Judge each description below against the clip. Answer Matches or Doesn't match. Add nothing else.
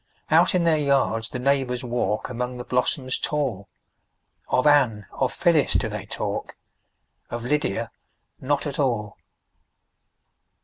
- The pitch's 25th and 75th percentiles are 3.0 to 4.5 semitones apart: Matches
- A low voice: Matches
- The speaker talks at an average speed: Doesn't match